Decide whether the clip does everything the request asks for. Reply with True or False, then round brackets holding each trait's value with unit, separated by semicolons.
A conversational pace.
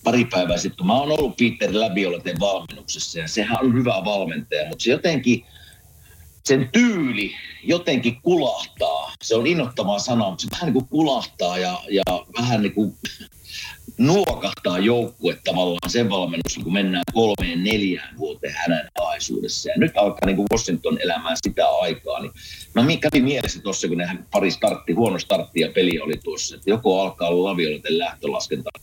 False (160 wpm)